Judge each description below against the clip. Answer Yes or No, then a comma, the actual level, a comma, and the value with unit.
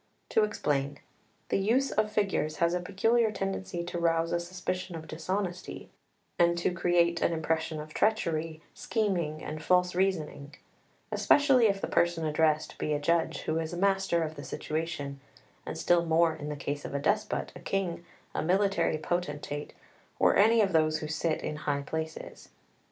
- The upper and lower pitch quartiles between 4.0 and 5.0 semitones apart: No, average, 3.6 semitones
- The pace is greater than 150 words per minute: Yes, average, 170 wpm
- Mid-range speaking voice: Yes, medium, 170 Hz